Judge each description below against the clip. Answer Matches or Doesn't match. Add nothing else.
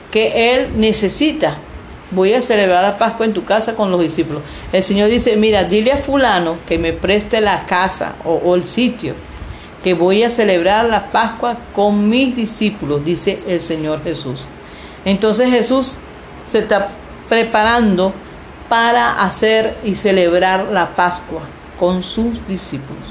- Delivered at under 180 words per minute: Matches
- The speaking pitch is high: Matches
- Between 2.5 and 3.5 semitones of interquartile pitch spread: Doesn't match